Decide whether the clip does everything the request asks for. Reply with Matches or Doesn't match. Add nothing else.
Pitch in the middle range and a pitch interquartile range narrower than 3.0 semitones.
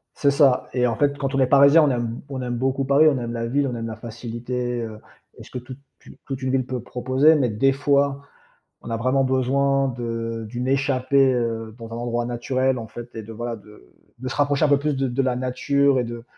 Doesn't match